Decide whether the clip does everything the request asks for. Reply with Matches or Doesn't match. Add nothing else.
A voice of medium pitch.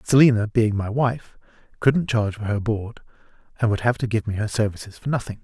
Doesn't match